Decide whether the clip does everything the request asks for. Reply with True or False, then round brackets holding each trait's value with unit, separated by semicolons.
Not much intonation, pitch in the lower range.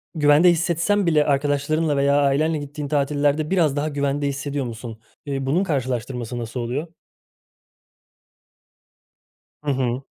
False (2.2 semitones; 145 Hz)